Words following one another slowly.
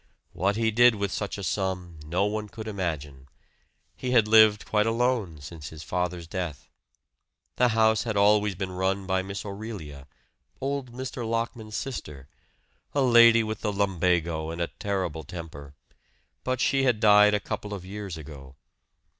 No: average, 160 wpm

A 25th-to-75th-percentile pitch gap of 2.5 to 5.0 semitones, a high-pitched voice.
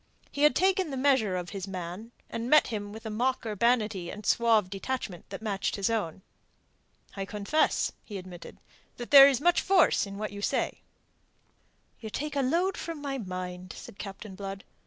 No: wide, 5.5 semitones; high, 215 Hz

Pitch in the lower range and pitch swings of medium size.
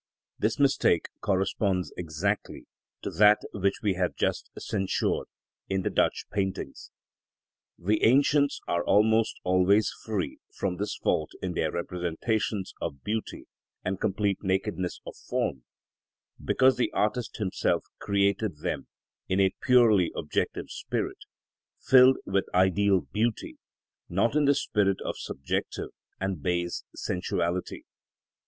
Yes: low, 100 Hz; average, 3.1 semitones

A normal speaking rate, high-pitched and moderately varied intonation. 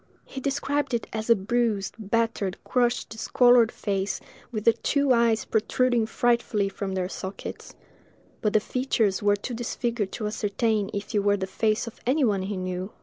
Yes: average, 170 wpm; high, 220 Hz; average, 3.0 semitones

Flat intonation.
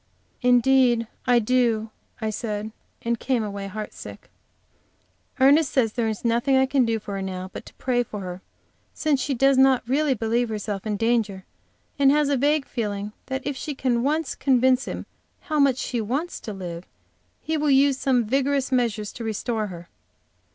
No: average, 3.9 semitones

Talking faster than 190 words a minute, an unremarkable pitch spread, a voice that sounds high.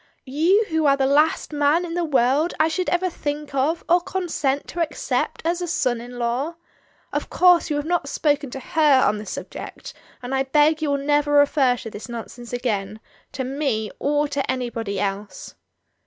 Yes: average, 200 wpm; average, 4.3 semitones; very high, 285 Hz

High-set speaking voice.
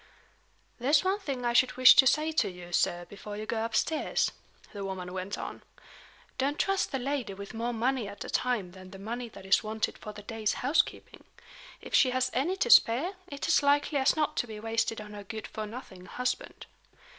Yes: high, 230 Hz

